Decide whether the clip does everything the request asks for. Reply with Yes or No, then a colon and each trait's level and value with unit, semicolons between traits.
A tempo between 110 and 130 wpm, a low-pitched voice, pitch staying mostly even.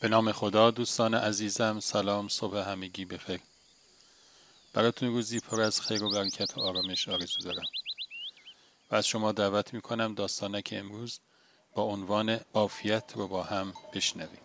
No: average, 145 wpm; low, 105 Hz; narrow, 1.9 semitones